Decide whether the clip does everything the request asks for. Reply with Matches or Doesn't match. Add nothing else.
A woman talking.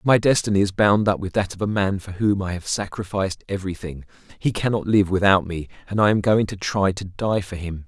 Doesn't match